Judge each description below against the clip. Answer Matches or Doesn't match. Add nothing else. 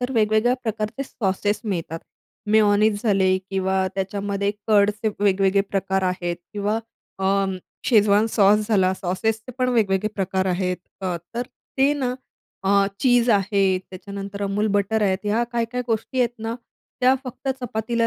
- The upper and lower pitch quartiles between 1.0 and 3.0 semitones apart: Matches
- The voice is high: Matches